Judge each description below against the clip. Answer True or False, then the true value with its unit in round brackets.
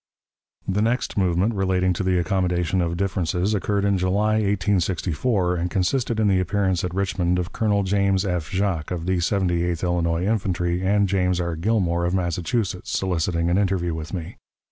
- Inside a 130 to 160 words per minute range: False (170 wpm)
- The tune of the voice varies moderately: False (2.2 semitones)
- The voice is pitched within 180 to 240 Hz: False (95 Hz)